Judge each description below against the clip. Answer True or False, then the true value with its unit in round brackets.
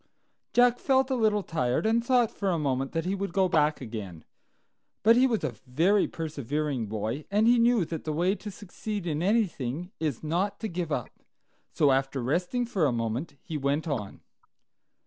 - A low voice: False (165 Hz)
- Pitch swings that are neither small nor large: False (7.2 semitones)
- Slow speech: False (185 wpm)